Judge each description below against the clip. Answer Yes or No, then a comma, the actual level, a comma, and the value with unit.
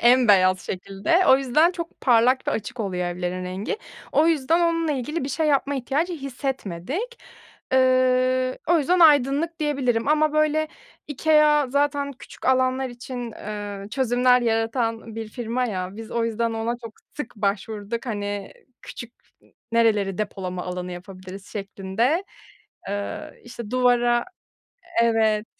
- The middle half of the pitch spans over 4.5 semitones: Yes, average, 5.2 semitones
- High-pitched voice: Yes, high, 240 Hz